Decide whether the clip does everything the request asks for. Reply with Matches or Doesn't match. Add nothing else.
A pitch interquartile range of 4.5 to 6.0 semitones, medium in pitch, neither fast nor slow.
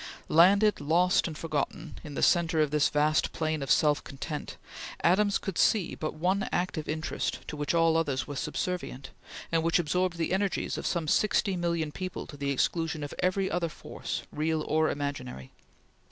Doesn't match